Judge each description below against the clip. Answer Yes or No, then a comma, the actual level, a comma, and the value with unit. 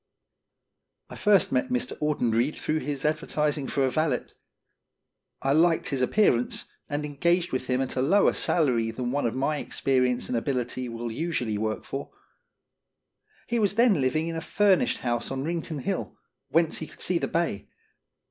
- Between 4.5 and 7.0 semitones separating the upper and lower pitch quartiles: Yes, average, 4.8 semitones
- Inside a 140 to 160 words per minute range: No, average, 170 wpm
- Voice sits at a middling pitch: Yes, medium, 145 Hz